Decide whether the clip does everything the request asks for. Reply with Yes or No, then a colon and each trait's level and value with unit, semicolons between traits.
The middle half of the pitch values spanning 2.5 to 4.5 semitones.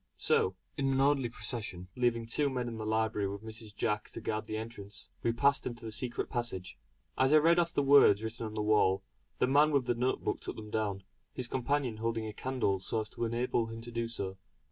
Yes: average, 2.9 semitones